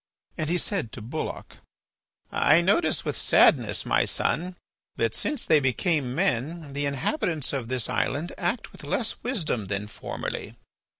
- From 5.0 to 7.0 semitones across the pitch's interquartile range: Yes, wide, 5.6 semitones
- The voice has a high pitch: No, medium, 155 Hz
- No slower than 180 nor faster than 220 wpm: No, average, 145 wpm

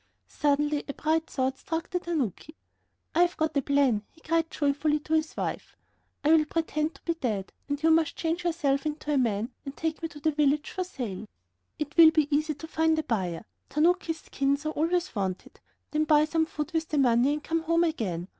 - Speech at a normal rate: No, fast, 210 wpm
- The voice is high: Yes, very high, 305 Hz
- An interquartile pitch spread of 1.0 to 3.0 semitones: Yes, narrow, 2.5 semitones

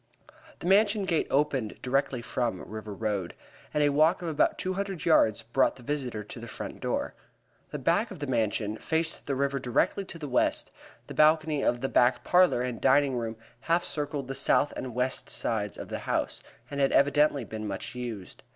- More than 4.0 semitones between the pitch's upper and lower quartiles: Yes, average, 4.7 semitones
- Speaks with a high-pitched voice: No, low, 135 Hz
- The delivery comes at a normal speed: Yes, average, 195 wpm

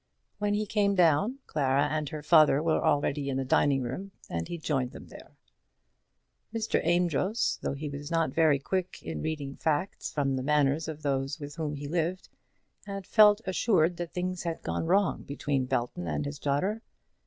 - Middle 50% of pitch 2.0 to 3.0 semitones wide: No, average, 4.5 semitones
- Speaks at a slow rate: No, average, 180 wpm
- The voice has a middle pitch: Yes, medium, 155 Hz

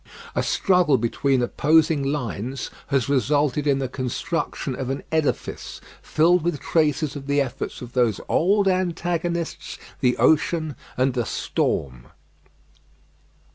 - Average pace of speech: No, slow, 125 wpm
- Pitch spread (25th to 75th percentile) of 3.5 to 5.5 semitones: Yes, average, 4.0 semitones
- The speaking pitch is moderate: Yes, medium, 145 Hz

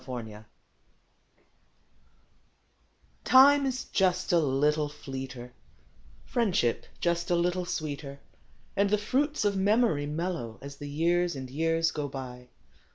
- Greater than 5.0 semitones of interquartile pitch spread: Yes, wide, 5.4 semitones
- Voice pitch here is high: No, medium, 160 Hz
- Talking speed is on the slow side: Yes, slow, 125 wpm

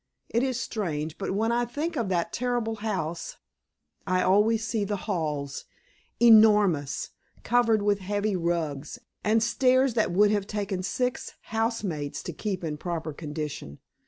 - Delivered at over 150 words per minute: No, average, 145 wpm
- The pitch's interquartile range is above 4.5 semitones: Yes, average, 5.0 semitones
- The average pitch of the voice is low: No, high, 205 Hz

